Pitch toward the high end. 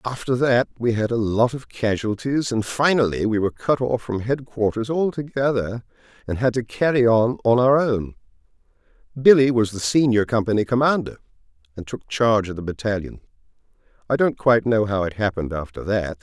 No: low, 115 Hz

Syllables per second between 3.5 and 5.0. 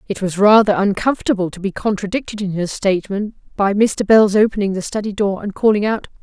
No: 5.9 syllables/s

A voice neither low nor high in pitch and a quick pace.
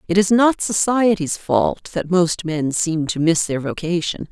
No: medium, 170 Hz; average, 180 wpm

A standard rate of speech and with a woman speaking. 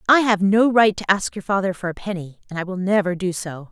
No: fast, 275 wpm; female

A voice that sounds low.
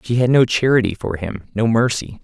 Yes: low, 110 Hz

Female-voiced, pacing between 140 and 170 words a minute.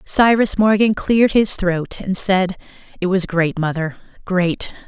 Yes: female; average, 150 wpm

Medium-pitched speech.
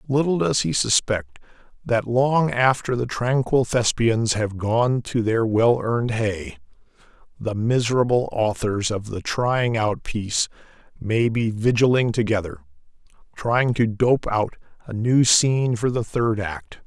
No: low, 115 Hz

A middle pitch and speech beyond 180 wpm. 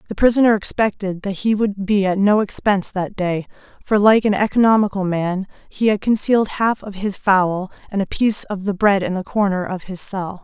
No: high, 200 Hz; fast, 205 wpm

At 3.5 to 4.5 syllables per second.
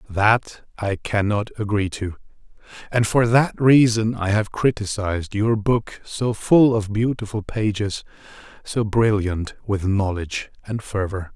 Yes: 4.0 syllables/s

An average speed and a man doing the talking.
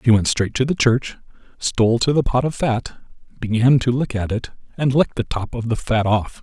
No: fast, 235 wpm; male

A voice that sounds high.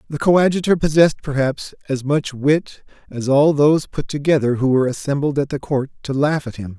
No: medium, 140 Hz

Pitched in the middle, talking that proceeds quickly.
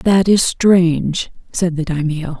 No: medium, 170 Hz; average, 150 wpm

